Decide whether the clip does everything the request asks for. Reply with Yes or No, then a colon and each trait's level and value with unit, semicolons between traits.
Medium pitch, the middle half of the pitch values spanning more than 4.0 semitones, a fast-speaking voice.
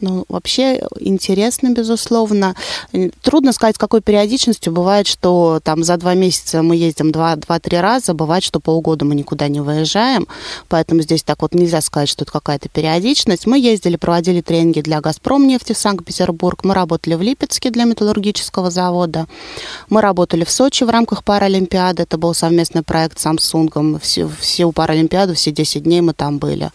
Yes: medium, 175 Hz; average, 4.5 semitones; fast, 170 wpm